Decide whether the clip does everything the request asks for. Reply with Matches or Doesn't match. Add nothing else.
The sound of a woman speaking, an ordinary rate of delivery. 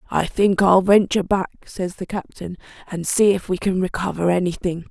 Matches